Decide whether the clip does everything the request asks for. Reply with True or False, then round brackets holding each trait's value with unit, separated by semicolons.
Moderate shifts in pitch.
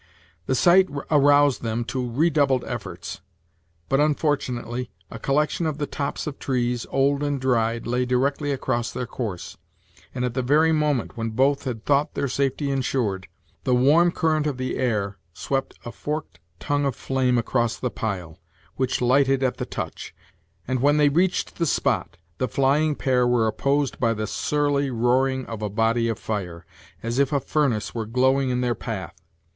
True (3.3 semitones)